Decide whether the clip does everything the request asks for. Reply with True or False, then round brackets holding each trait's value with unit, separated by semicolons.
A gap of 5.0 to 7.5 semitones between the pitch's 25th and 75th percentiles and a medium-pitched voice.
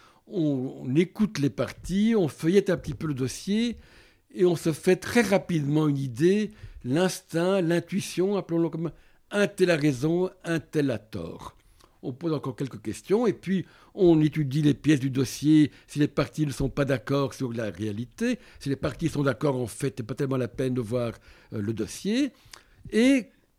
True (5.3 semitones; 150 Hz)